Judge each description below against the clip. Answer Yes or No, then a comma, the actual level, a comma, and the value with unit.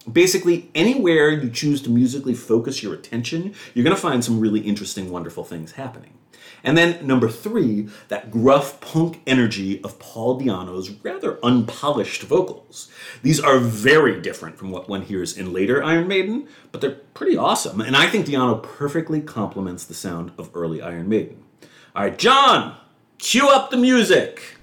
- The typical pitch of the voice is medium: No, low, 125 Hz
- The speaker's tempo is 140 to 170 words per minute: Yes, average, 165 wpm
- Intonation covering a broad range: Yes, wide, 8.2 semitones